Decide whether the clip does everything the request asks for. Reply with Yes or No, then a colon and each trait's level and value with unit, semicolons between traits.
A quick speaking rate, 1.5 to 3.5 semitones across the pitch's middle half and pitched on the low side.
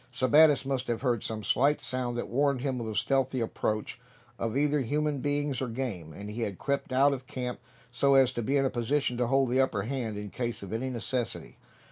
Yes: fast, 220 wpm; average, 2.9 semitones; low, 130 Hz